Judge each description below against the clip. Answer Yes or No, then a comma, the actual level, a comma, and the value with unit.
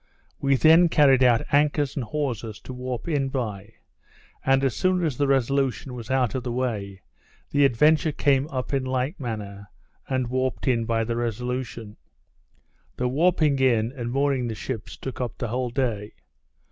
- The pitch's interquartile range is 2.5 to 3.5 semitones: Yes, average, 2.9 semitones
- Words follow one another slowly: No, average, 170 wpm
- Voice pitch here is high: No, low, 130 Hz